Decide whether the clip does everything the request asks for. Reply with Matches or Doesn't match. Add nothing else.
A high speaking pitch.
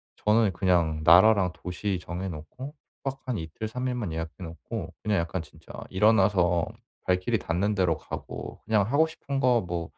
Doesn't match